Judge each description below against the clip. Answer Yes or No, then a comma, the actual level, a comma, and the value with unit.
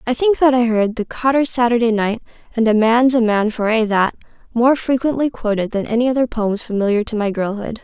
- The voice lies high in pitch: Yes, high, 230 Hz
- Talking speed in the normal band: No, fast, 215 wpm